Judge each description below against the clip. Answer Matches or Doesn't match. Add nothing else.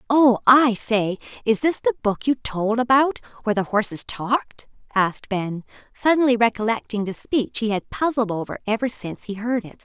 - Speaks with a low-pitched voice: Doesn't match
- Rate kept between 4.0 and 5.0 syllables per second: Doesn't match